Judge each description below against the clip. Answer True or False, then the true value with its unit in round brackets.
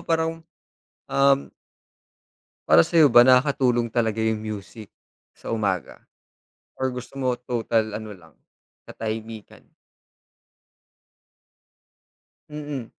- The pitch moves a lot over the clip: False (3.7 semitones)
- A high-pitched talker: False (120 Hz)